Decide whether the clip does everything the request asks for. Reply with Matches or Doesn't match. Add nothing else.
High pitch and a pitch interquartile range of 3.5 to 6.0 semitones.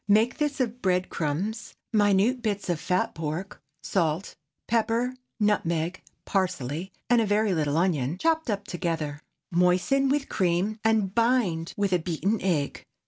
Matches